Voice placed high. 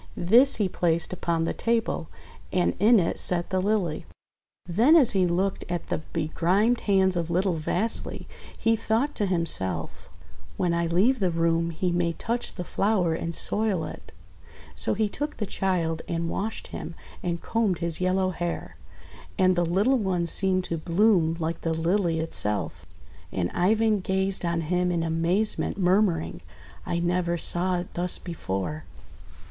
No: medium, 180 Hz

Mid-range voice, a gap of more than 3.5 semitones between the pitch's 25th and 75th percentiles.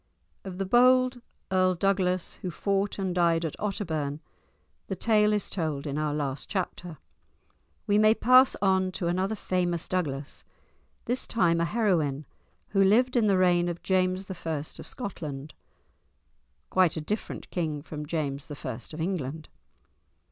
Yes: medium, 180 Hz; average, 4.1 semitones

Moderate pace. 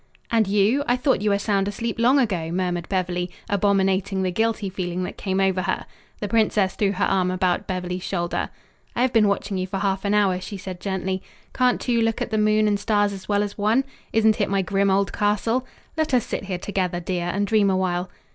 No: fast, 220 wpm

